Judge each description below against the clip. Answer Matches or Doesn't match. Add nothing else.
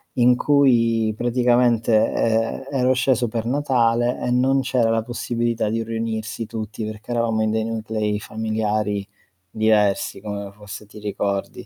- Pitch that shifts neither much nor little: Doesn't match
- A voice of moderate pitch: Doesn't match